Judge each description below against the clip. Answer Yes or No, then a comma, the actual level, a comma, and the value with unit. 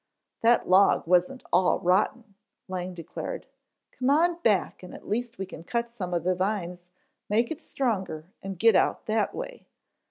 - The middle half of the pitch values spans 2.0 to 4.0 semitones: No, average, 4.7 semitones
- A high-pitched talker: Yes, high, 200 Hz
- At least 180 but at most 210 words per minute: No, average, 165 wpm